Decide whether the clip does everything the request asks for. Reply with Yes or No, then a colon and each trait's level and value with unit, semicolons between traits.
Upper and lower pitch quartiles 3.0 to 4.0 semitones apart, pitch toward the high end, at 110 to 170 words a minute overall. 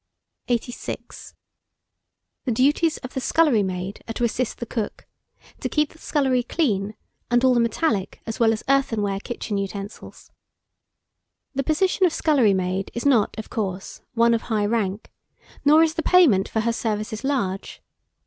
No: average, 5.0 semitones; high, 235 Hz; average, 160 wpm